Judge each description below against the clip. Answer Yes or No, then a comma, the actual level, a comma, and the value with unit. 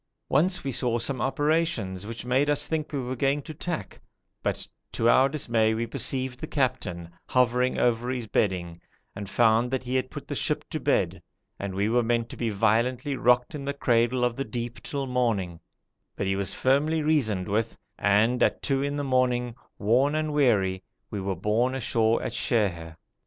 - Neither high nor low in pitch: No, low, 125 Hz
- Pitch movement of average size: Yes, average, 3.8 semitones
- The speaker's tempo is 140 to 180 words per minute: No, average, 190 wpm